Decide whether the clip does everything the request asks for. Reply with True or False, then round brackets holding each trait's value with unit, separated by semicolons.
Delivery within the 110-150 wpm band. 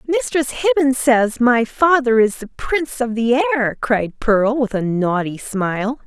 False (170 wpm)